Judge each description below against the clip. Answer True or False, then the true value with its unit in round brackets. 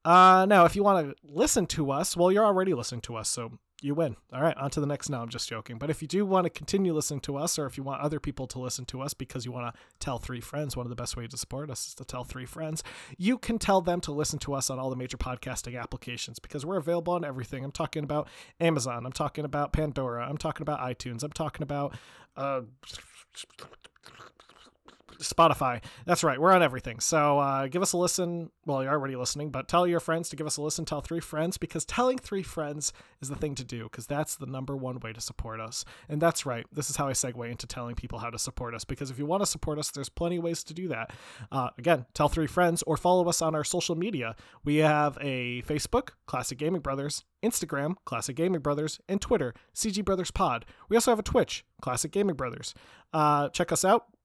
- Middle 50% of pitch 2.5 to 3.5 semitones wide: False (4.6 semitones)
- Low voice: False (150 Hz)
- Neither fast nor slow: False (240 wpm)